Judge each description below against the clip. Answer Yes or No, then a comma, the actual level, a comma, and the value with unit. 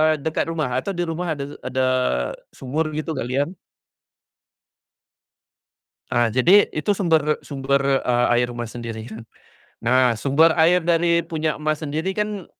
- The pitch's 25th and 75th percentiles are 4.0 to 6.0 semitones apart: Yes, average, 4.5 semitones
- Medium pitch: Yes, medium, 150 Hz